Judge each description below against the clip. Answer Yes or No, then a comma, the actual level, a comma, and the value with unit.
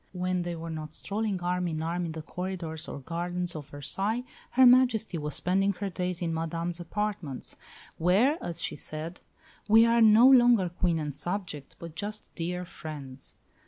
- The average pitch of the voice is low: No, medium, 175 Hz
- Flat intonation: No, average, 3.9 semitones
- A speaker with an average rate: Yes, average, 170 wpm